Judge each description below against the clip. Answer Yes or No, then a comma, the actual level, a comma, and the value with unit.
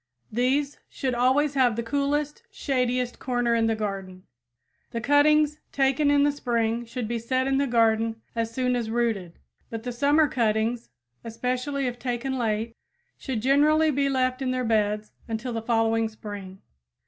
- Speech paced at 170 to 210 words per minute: No, average, 160 wpm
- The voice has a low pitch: No, high, 245 Hz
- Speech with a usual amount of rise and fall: Yes, average, 3.2 semitones